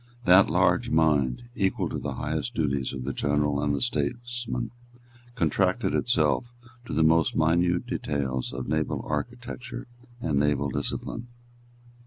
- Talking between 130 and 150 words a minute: Yes, slow, 135 wpm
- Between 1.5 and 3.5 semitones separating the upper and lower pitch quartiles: No, wide, 5.6 semitones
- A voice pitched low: Yes, very low, 80 Hz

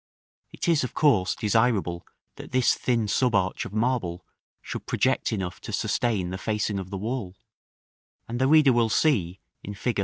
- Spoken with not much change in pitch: No, average, 4.8 semitones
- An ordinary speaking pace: Yes, average, 175 wpm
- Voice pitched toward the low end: Yes, low, 110 Hz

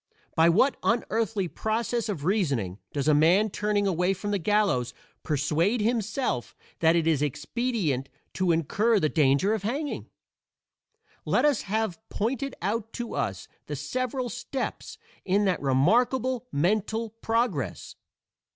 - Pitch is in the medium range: No, high, 205 Hz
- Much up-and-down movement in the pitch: Yes, wide, 6.2 semitones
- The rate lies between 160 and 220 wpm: No, slow, 135 wpm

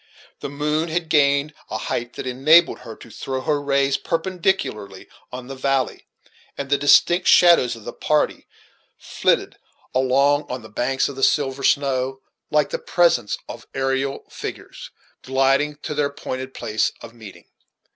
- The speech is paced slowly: No, average, 155 wpm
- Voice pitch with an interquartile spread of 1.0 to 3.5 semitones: Yes, narrow, 2.6 semitones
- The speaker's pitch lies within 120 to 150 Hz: Yes, low, 135 Hz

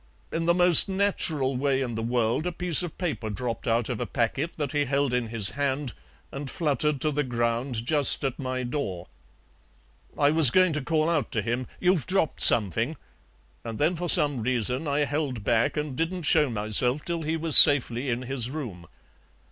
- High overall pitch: No, medium, 140 Hz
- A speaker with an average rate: Yes, average, 190 wpm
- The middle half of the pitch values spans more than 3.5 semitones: Yes, average, 4.7 semitones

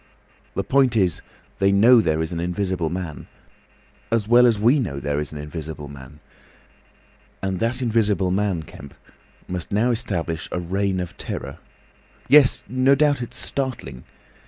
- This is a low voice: Yes, very low, 95 Hz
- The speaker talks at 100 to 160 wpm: Yes, average, 150 wpm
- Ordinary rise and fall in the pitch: No, wide, 6.4 semitones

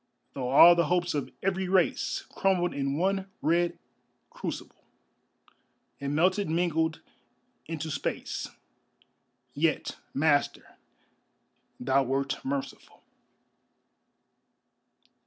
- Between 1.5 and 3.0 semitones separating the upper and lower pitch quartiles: No, average, 4.1 semitones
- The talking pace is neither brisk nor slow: No, slow, 85 wpm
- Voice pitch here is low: No, medium, 160 Hz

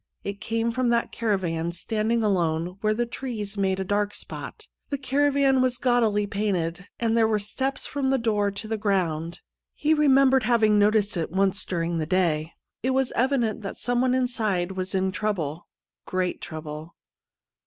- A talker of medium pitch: No, high, 210 Hz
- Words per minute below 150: No, average, 170 wpm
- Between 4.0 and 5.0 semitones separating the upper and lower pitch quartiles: Yes, average, 4.6 semitones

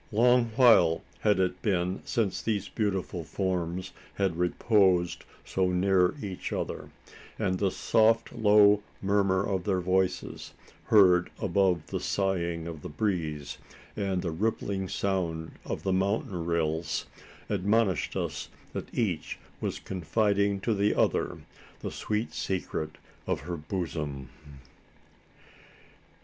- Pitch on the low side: Yes, very low, 95 Hz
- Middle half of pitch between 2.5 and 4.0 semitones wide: Yes, average, 2.9 semitones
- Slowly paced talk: Yes, slow, 120 wpm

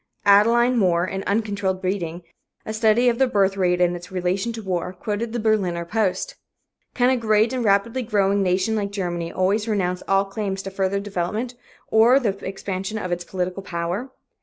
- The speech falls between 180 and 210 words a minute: Yes, average, 185 wpm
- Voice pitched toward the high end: Yes, high, 200 Hz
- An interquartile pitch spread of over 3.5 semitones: No, average, 3.1 semitones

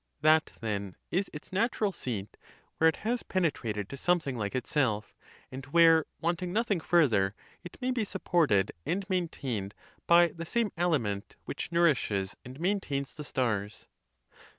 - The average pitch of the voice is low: No, medium, 155 Hz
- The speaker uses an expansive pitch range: Yes, wide, 7.8 semitones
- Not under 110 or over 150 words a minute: Yes, average, 145 wpm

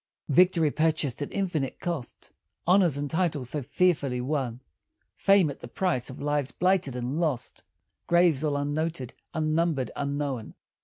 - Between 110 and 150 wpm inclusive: Yes, average, 140 wpm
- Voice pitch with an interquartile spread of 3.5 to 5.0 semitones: Yes, average, 4.1 semitones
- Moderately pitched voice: Yes, medium, 150 Hz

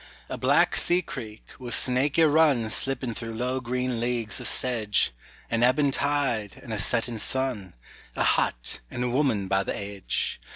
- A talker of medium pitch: No, low, 125 Hz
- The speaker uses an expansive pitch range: No, average, 3.3 semitones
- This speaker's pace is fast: No, average, 165 wpm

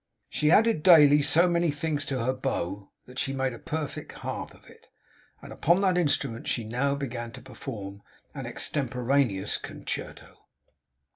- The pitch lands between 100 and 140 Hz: Yes, low, 135 Hz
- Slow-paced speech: No, average, 155 wpm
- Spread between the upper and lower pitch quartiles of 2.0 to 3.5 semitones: No, average, 4.3 semitones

